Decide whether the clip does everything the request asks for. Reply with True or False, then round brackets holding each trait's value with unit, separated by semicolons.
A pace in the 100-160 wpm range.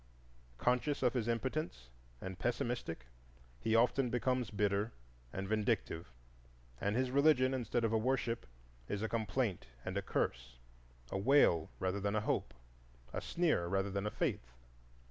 True (145 wpm)